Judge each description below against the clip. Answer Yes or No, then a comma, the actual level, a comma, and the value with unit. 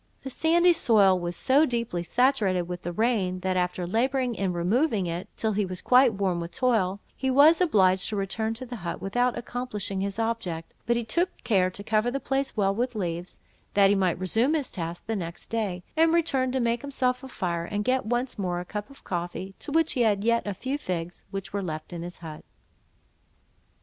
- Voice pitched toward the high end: Yes, high, 210 Hz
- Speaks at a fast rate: Yes, fast, 210 wpm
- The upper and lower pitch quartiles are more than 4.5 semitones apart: Yes, wide, 5.5 semitones